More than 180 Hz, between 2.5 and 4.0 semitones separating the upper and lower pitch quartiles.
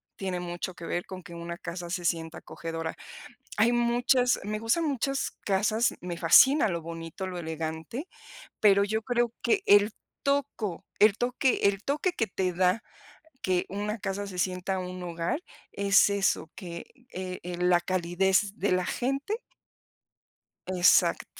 No: high, 190 Hz; average, 4.4 semitones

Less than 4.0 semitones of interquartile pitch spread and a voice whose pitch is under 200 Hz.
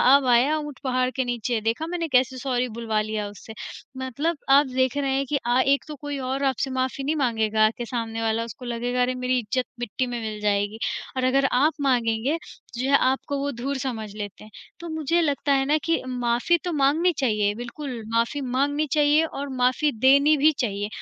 No: average, 3.3 semitones; very high, 255 Hz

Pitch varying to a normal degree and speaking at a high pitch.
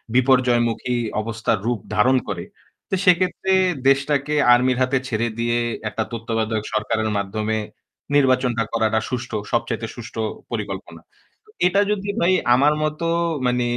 No: average, 3.3 semitones; low, 120 Hz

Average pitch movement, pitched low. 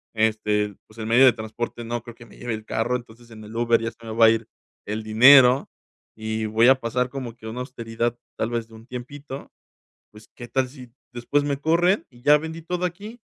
Yes: average, 3.0 semitones; low, 120 Hz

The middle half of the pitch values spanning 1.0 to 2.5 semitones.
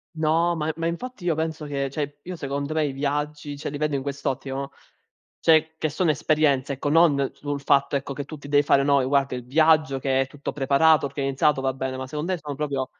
Yes: narrow, 2.1 semitones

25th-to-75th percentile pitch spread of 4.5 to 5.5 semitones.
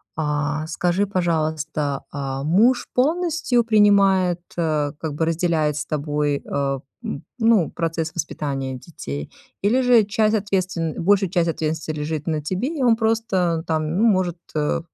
Yes: average, 5.2 semitones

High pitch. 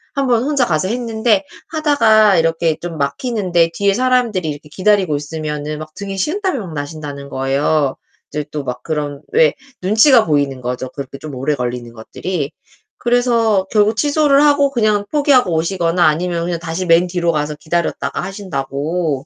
No: medium, 175 Hz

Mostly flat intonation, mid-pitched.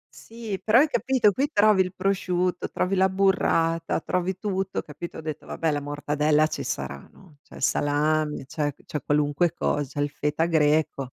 No: average, 4.4 semitones; medium, 165 Hz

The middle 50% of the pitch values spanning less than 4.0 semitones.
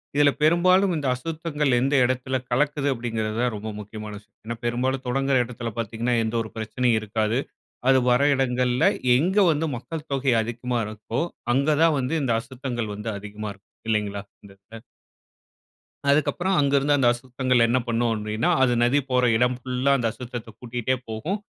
Yes: average, 3.6 semitones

